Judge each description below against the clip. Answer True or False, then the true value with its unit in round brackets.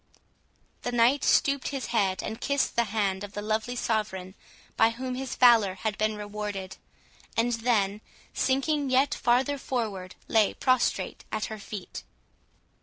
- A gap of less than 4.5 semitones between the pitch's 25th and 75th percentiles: True (3.6 semitones)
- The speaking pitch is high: True (225 Hz)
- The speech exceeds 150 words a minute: False (145 wpm)